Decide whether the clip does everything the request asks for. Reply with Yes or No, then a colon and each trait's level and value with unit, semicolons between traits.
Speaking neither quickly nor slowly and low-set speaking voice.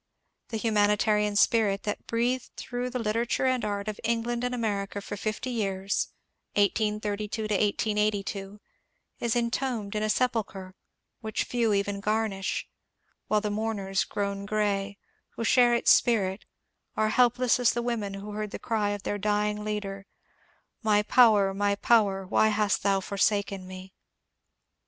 No: average, 145 wpm; high, 210 Hz